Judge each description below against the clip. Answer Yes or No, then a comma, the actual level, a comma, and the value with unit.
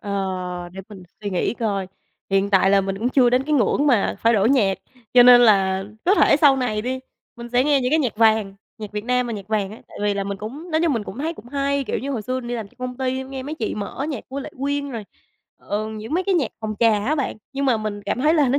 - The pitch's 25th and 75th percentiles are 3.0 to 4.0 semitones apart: No, average, 4.8 semitones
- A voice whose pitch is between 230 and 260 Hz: Yes, high, 235 Hz